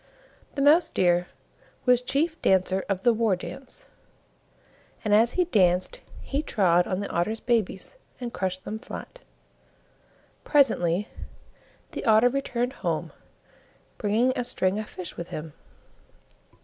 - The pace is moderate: No, slow, 130 wpm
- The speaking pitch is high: Yes, high, 215 Hz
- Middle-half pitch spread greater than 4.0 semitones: Yes, average, 5.3 semitones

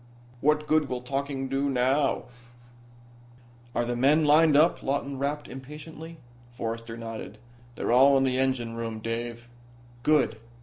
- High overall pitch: No, low, 135 Hz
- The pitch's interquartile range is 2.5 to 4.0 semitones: Yes, average, 3.6 semitones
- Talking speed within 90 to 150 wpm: Yes, slow, 135 wpm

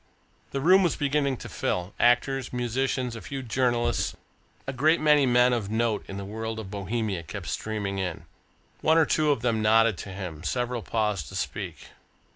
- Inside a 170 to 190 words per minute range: Yes, average, 180 wpm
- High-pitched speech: No, low, 120 Hz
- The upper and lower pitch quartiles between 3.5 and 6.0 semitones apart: Yes, average, 4.3 semitones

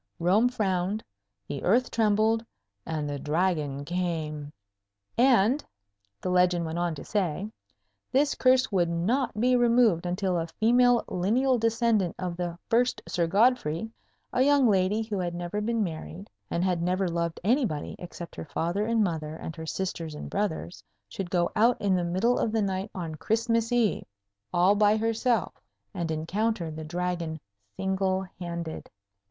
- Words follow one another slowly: No, average, 155 wpm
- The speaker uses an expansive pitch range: No, average, 4.9 semitones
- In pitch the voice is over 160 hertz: Yes, high, 190 Hz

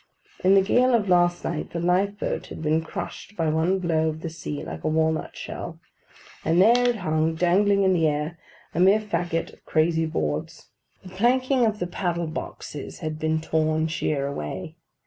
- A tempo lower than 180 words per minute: No, average, 185 wpm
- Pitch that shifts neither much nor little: Yes, average, 3.5 semitones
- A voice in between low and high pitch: Yes, medium, 170 Hz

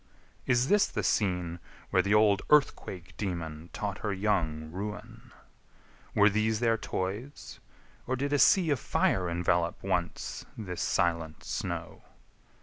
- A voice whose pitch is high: No, low, 100 Hz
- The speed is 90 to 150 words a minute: Yes, slow, 135 wpm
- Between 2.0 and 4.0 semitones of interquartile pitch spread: No, average, 4.6 semitones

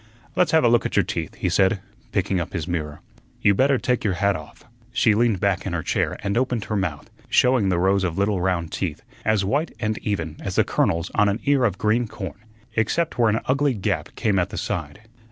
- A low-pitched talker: Yes, low, 100 Hz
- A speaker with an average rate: No, fast, 225 wpm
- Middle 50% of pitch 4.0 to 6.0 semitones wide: Yes, average, 4.4 semitones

